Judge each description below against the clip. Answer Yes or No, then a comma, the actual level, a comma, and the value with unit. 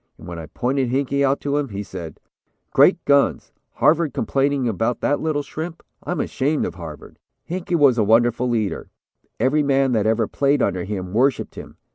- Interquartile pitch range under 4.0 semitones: No, average, 4.8 semitones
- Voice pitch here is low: Yes, low, 130 Hz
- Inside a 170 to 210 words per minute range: Yes, average, 180 wpm